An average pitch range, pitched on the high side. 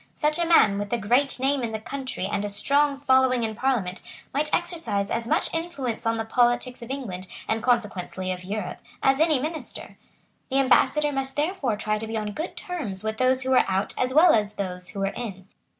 Yes: average, 4.9 semitones; high, 245 Hz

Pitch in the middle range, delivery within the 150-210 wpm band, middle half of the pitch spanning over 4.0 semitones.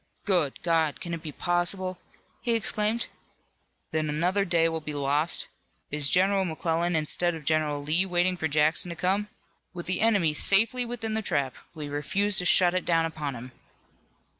No: medium, 170 Hz; average, 170 wpm; average, 3.7 semitones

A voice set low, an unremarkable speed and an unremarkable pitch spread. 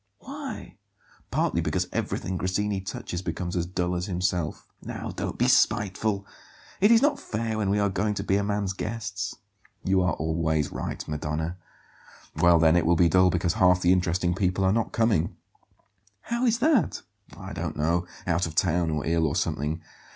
Yes: very low, 90 Hz; average, 180 wpm; average, 3.4 semitones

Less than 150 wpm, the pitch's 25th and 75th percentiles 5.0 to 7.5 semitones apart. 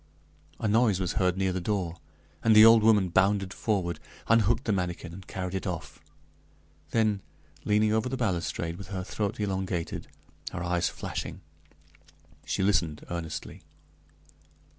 No: average, 140 wpm; average, 3.3 semitones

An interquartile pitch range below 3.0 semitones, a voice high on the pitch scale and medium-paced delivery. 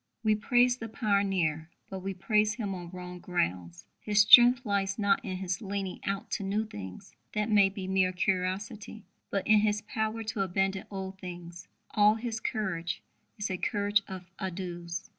Yes: narrow, 2.5 semitones; high, 195 Hz; average, 170 wpm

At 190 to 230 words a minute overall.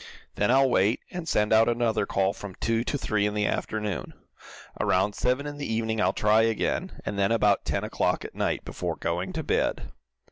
Yes: average, 200 wpm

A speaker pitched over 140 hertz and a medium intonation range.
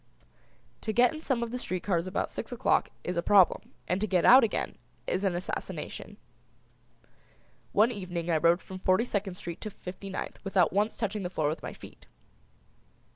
Yes: high, 190 Hz; average, 3.2 semitones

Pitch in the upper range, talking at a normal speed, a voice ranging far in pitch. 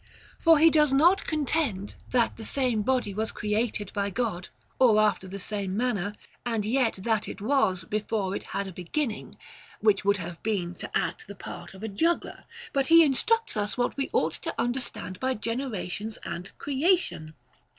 No: high, 220 Hz; average, 185 wpm; average, 5.0 semitones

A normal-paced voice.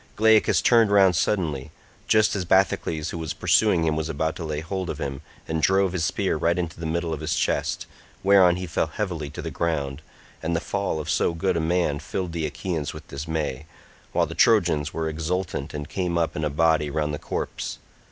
No: fast, 210 wpm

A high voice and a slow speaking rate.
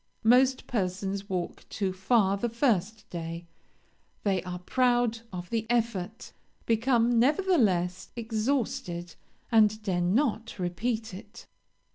Yes: high, 215 Hz; slow, 110 wpm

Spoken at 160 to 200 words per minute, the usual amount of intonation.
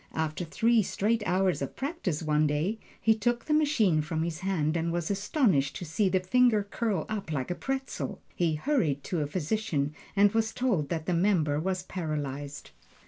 No: average, 185 wpm; wide, 6.0 semitones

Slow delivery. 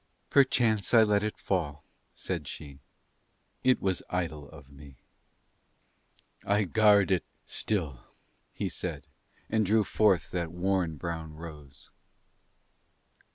Yes: slow, 110 wpm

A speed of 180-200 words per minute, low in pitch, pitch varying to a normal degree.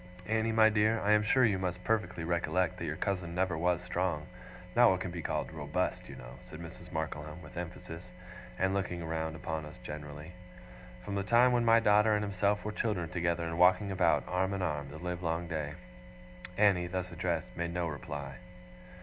Yes: average, 195 wpm; very low, 90 Hz; average, 3.4 semitones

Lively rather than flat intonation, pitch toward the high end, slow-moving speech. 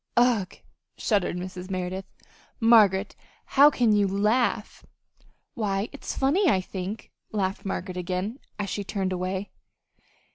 No: average, 3.3 semitones; high, 200 Hz; slow, 130 wpm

